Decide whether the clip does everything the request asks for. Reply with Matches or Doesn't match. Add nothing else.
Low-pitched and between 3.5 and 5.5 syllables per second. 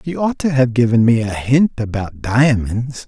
Matches